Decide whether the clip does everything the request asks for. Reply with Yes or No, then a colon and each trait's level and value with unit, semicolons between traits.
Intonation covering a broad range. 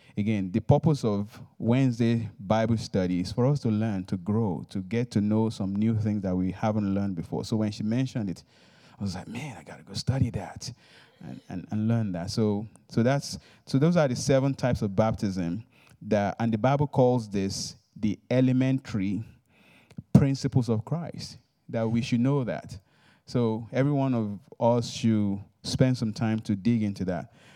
No: average, 3.6 semitones